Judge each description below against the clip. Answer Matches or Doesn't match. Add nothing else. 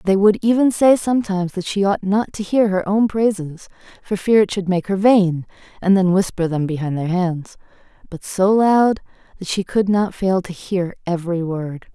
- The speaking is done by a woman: Matches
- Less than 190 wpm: Doesn't match